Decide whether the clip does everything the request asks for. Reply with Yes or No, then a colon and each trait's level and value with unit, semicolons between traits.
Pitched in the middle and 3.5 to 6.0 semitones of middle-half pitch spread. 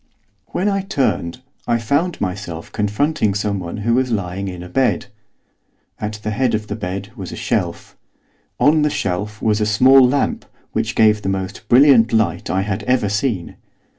No: low, 110 Hz; average, 4.6 semitones